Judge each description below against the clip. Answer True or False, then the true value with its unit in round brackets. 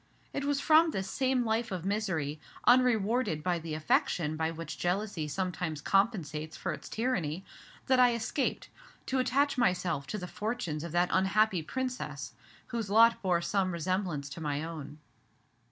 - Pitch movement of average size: False (6.5 semitones)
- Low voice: False (190 Hz)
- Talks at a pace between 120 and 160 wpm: True (155 wpm)